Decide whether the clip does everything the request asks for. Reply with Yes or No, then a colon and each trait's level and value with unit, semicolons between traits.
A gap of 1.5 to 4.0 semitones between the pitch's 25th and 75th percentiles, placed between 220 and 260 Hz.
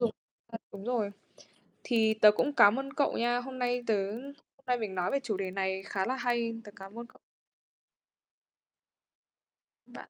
Yes: average, 3.7 semitones; high, 230 Hz